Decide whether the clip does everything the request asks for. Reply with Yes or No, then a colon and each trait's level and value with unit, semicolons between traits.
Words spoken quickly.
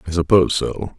No: average, 185 wpm